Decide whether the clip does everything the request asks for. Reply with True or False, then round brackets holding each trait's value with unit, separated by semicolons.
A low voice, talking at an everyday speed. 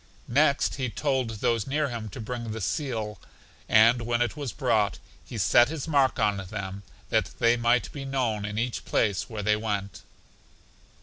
True (115 Hz; 175 wpm)